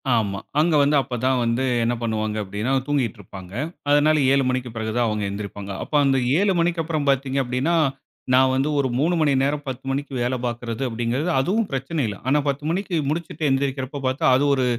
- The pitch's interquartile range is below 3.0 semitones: No, average, 4.0 semitones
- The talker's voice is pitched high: No, low, 130 Hz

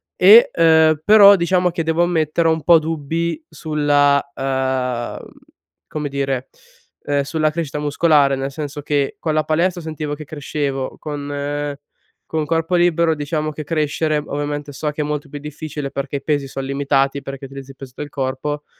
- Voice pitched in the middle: Yes, medium, 150 Hz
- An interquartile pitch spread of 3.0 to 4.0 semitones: No, narrow, 2.4 semitones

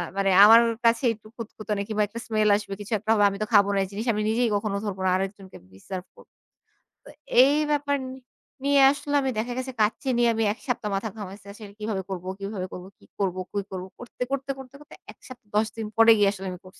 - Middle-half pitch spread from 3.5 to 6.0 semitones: No, average, 3.1 semitones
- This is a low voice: No, high, 215 Hz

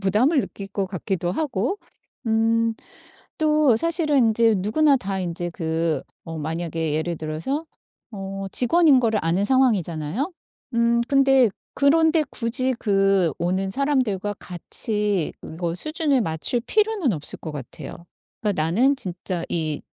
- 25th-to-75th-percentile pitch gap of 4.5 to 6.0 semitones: No, wide, 7.4 semitones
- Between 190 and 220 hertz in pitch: Yes, high, 210 Hz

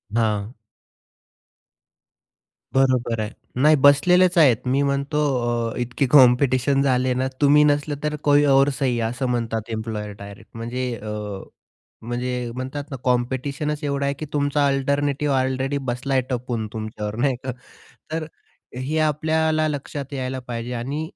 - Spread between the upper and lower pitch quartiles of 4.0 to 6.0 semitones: No, average, 2.9 semitones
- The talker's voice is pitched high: No, low, 135 Hz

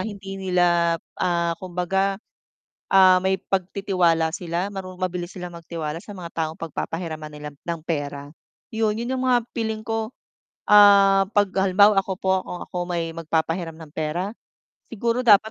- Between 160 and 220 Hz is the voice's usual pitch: Yes, medium, 185 Hz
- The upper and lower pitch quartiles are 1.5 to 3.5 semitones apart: Yes, average, 3.0 semitones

